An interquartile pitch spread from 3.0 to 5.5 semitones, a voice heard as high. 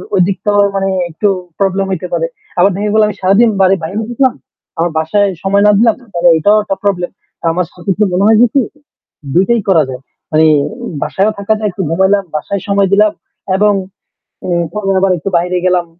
No: narrow, 2.5 semitones; high, 195 Hz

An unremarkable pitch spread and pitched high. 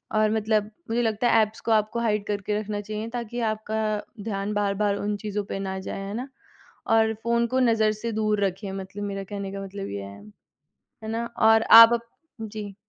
No: narrow, 1.8 semitones; high, 215 Hz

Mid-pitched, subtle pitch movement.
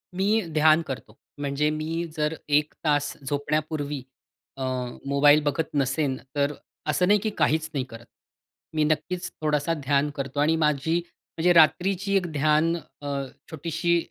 Yes: medium, 150 Hz; narrow, 2.2 semitones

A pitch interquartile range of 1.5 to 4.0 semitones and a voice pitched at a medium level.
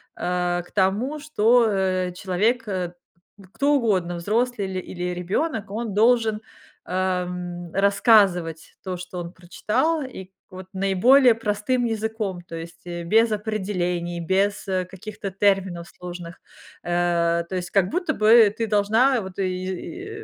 No: average, 3.7 semitones; high, 195 Hz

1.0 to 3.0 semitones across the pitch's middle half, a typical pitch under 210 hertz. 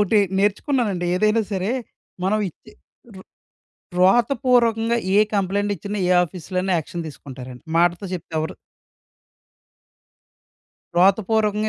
No: average, 3.5 semitones; high, 195 Hz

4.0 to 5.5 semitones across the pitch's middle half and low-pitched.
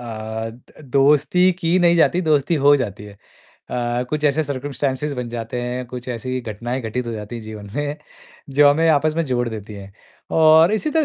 Yes: average, 4.5 semitones; low, 130 Hz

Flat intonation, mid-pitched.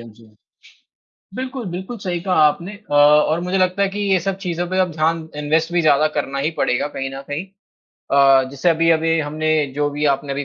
No: average, 3.9 semitones; medium, 160 Hz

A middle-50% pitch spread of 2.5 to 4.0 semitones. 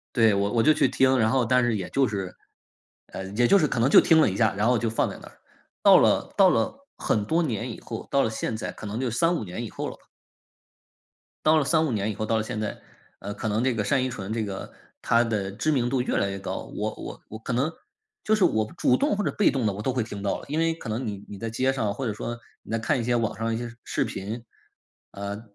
Yes: average, 3.7 semitones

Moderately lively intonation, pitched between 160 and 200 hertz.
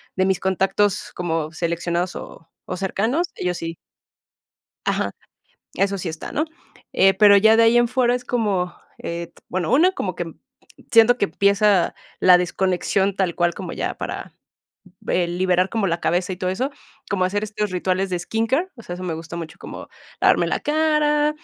Yes: average, 4.0 semitones; high, 190 Hz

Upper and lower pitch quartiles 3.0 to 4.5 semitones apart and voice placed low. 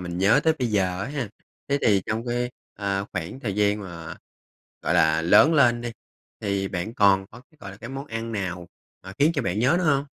Yes: average, 4.1 semitones; low, 105 Hz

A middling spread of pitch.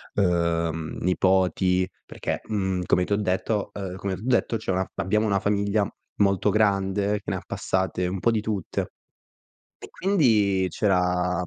No: narrow, 2.2 semitones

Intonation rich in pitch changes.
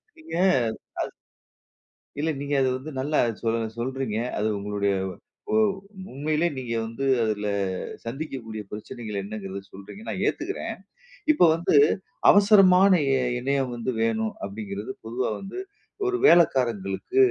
Yes: wide, 6.3 semitones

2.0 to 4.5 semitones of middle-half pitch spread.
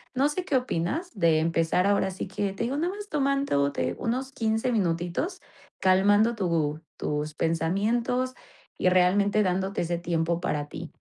No: wide, 6.8 semitones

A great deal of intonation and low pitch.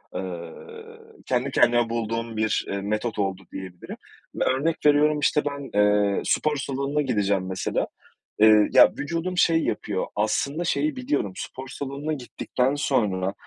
Yes: wide, 6.4 semitones; low, 125 Hz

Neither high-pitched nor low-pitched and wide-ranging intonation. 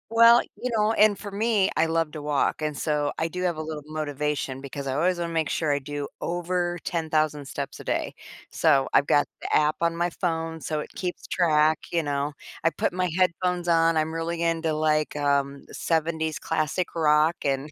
No: medium, 160 Hz; narrow, 2.5 semitones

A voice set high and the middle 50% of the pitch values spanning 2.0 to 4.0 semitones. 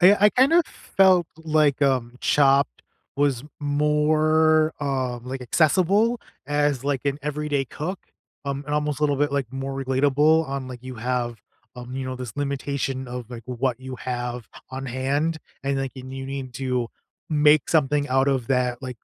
No: medium, 140 Hz; narrow, 2.6 semitones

